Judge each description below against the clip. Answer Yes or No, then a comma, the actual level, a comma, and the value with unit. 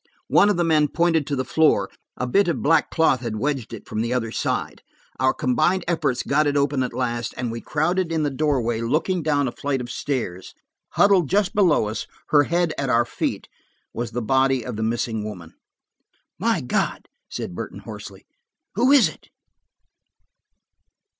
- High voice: No, medium, 140 Hz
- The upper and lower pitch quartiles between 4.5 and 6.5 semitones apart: Yes, average, 5.3 semitones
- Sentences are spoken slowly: No, average, 180 wpm